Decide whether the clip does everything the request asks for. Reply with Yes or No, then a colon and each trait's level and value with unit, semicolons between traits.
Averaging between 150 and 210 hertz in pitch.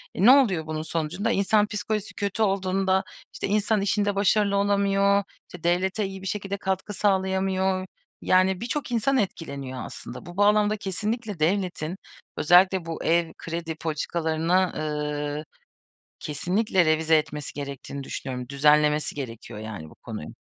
Yes: medium, 185 Hz